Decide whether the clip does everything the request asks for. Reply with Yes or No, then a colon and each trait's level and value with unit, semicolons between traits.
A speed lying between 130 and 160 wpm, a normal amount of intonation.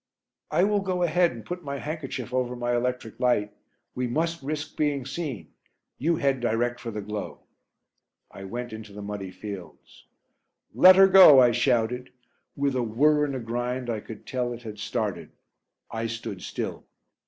No: average, 170 wpm; average, 4.6 semitones